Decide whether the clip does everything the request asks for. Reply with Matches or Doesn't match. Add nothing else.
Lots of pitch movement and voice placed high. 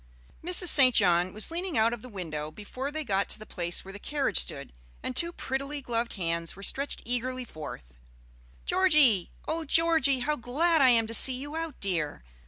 Matches